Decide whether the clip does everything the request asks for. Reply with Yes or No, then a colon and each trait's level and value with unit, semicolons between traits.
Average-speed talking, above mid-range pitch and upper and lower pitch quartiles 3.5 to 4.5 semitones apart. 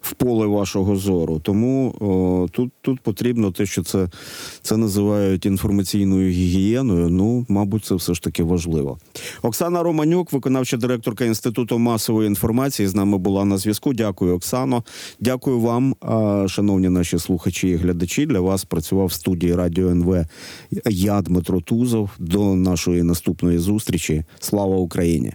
No: average, 140 wpm; low, 100 Hz; average, 4.1 semitones